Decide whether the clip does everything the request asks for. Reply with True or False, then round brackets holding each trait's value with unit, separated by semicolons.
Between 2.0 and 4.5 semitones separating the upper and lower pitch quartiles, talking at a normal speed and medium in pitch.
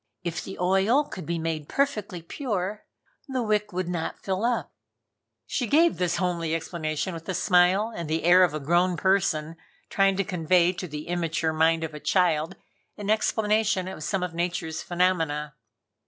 True (3.2 semitones; 170 wpm; 180 Hz)